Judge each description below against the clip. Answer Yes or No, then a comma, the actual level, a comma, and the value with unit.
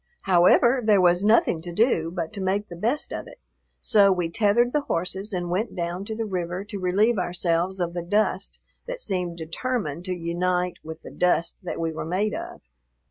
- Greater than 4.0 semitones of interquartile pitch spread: No, average, 3.4 semitones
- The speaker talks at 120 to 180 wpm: No, average, 195 wpm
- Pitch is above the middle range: No, medium, 180 Hz